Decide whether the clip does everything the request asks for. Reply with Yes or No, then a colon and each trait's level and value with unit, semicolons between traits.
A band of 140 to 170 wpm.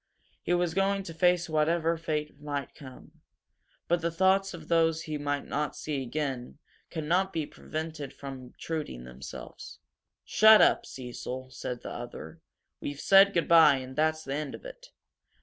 Yes: average, 155 wpm